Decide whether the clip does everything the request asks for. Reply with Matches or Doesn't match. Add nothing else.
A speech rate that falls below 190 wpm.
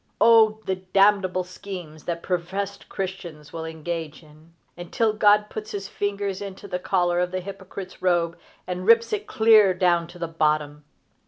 Matches